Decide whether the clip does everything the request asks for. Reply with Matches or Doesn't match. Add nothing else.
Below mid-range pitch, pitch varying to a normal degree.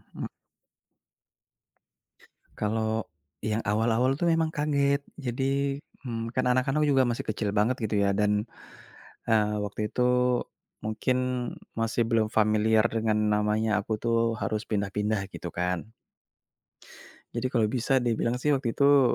Matches